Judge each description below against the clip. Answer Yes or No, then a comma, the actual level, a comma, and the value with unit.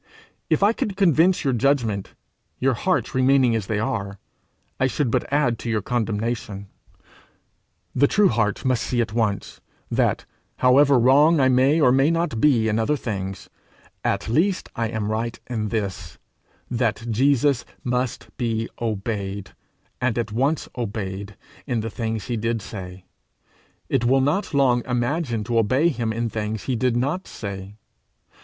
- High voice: No, low, 120 Hz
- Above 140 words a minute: Yes, average, 155 wpm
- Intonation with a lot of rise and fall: No, average, 3.7 semitones